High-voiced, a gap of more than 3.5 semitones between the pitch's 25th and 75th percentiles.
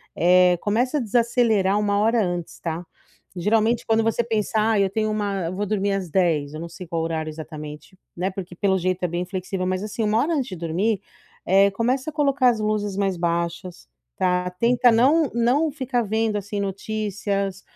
Yes: high, 200 Hz; average, 3.9 semitones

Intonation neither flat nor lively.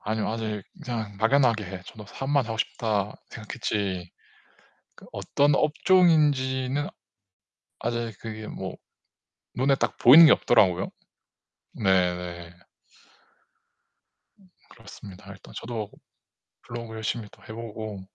Yes: average, 4.0 semitones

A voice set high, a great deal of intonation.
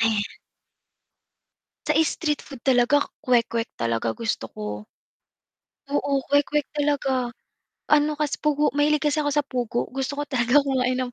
No: very high, 270 Hz; average, 3.8 semitones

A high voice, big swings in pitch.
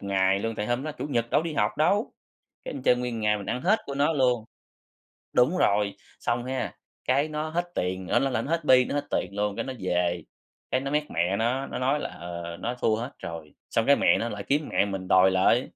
No: low, 120 Hz; wide, 6.2 semitones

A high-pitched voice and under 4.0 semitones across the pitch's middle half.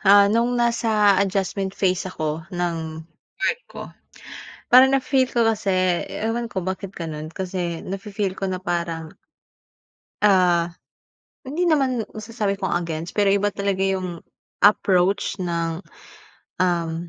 Yes: high, 195 Hz; average, 3.6 semitones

